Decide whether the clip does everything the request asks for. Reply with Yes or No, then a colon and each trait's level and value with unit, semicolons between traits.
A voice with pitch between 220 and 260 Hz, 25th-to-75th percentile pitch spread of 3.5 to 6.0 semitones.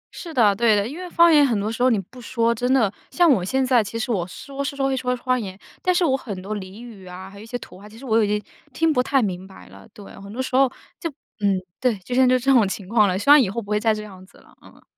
Yes: high, 230 Hz; average, 4.4 semitones